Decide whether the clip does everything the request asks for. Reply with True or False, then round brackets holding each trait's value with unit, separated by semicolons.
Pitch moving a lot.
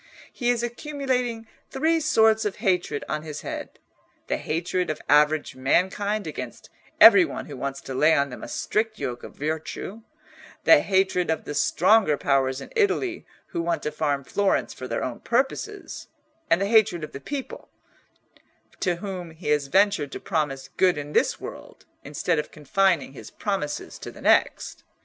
True (6.9 semitones)